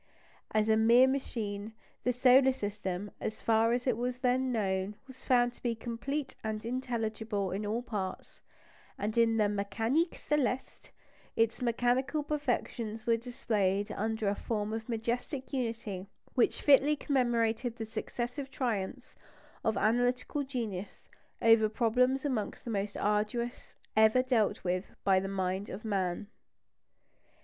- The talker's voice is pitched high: Yes, high, 230 Hz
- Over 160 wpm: No, average, 140 wpm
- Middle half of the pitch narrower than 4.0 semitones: Yes, average, 3.0 semitones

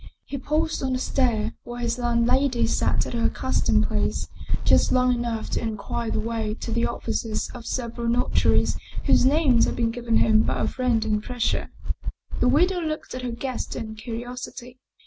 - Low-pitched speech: No, high, 240 Hz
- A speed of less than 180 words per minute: No, average, 185 wpm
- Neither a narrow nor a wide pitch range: No, narrow, 1.9 semitones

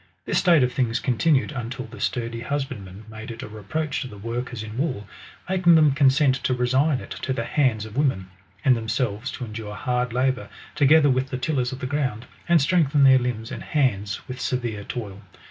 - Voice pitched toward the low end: Yes, low, 125 Hz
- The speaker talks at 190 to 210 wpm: Yes, average, 195 wpm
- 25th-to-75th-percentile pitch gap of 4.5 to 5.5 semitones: No, average, 3.5 semitones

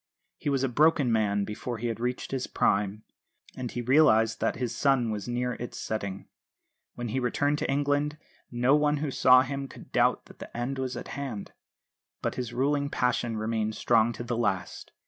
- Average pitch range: Yes, average, 3.4 semitones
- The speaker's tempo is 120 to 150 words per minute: No, average, 190 wpm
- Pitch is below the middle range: Yes, low, 125 Hz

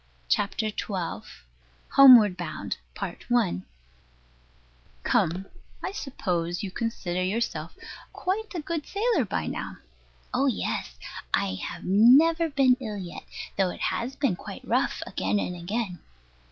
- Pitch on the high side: Yes, high, 210 Hz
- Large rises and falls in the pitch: Yes, wide, 7.3 semitones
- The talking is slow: Yes, slow, 120 wpm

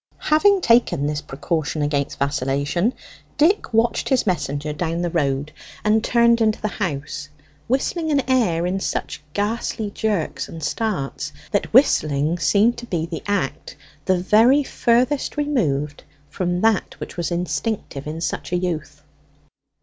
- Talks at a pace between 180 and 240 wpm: No, average, 140 wpm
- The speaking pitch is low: No, medium, 180 Hz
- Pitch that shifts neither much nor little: No, wide, 7.5 semitones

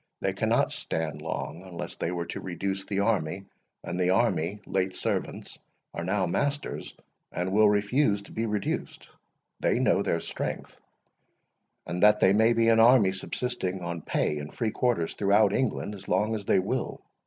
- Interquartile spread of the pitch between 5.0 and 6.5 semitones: No, average, 3.6 semitones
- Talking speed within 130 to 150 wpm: No, average, 170 wpm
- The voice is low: Yes, low, 100 Hz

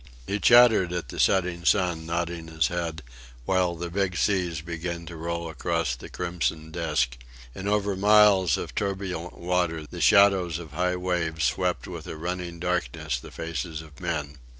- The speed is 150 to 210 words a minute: Yes, average, 165 wpm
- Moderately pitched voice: No, very low, 85 Hz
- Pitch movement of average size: No, narrow, 2.1 semitones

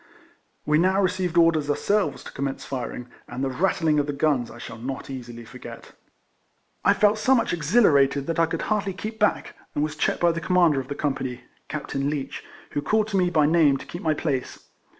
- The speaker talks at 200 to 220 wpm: Yes, fast, 205 wpm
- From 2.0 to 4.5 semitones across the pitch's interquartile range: No, average, 4.9 semitones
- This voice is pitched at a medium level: Yes, medium, 155 Hz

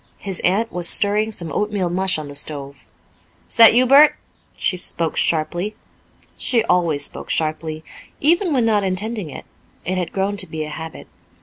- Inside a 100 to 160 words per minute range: No, average, 175 wpm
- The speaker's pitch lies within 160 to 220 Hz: Yes, medium, 185 Hz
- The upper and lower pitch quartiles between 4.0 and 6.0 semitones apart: Yes, average, 5.2 semitones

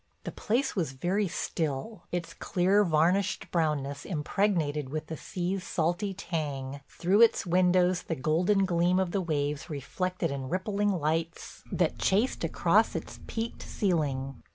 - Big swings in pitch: No, average, 4.1 semitones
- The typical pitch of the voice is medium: Yes, medium, 175 Hz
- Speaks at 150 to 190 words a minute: No, average, 140 wpm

